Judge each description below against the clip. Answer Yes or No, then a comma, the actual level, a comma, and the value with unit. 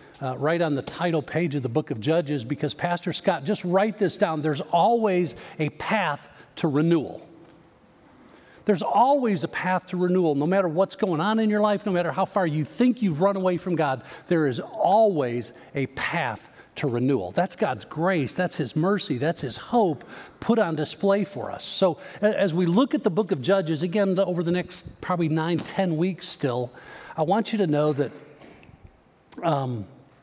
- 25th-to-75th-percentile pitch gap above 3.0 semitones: Yes, average, 4.7 semitones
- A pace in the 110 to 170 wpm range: No, average, 190 wpm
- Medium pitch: Yes, medium, 175 Hz